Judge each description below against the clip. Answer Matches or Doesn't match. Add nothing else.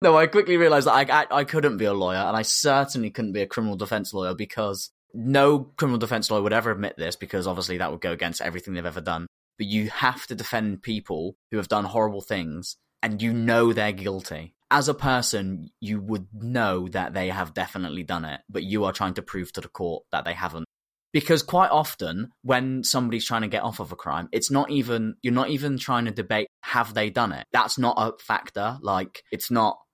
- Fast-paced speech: Matches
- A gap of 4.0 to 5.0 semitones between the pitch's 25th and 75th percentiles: Matches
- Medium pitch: Doesn't match